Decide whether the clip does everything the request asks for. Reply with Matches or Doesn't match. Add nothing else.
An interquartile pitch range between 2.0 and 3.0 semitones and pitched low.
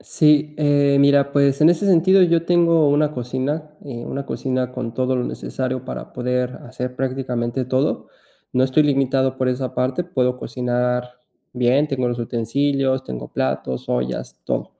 Matches